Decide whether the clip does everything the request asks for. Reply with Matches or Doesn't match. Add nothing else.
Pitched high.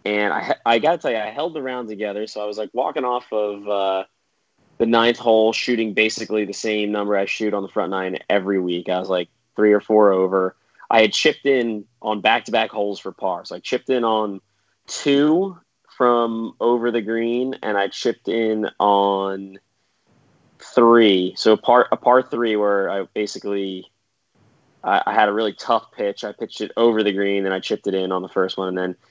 Doesn't match